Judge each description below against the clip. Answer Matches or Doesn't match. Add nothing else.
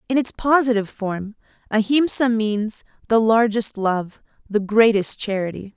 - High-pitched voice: Matches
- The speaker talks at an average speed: Doesn't match